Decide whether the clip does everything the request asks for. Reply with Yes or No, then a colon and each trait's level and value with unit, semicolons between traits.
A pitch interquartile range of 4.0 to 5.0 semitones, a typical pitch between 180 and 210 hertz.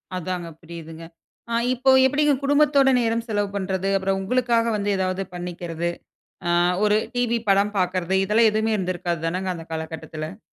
Yes: average, 4.6 semitones; high, 190 Hz